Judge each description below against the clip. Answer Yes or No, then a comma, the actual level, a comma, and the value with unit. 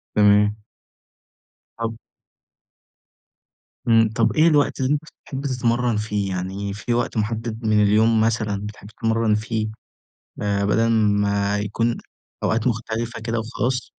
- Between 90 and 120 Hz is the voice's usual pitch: Yes, low, 110 Hz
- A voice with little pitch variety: Yes, narrow, 2.0 semitones